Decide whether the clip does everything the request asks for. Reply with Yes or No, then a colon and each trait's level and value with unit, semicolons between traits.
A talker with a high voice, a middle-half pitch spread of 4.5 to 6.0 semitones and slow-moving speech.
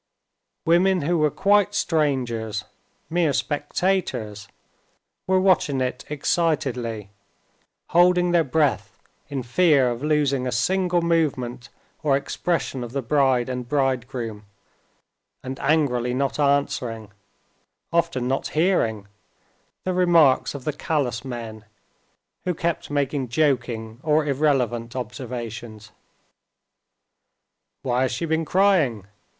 No: low, 135 Hz; average, 4.9 semitones; slow, 110 wpm